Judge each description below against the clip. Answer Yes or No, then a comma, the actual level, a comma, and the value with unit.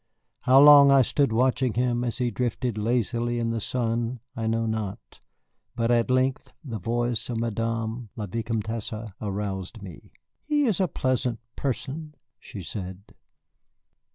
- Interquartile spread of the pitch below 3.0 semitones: Yes, narrow, 2.4 semitones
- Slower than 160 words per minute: Yes, average, 145 wpm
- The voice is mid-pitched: No, low, 115 Hz